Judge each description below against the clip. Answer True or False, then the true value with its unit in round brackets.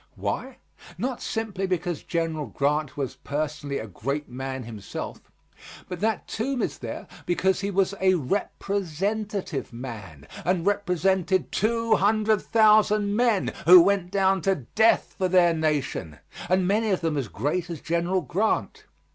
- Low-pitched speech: False (180 Hz)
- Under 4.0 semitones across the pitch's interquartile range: False (5.2 semitones)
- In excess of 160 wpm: False (145 wpm)